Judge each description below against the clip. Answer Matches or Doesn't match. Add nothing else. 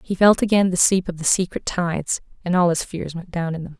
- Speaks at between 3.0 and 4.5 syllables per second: Doesn't match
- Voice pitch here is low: Doesn't match